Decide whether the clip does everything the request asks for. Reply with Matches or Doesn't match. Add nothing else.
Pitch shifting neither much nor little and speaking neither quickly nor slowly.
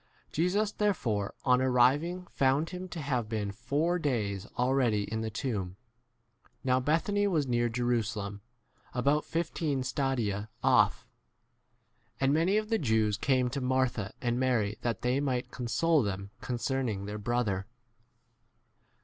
Matches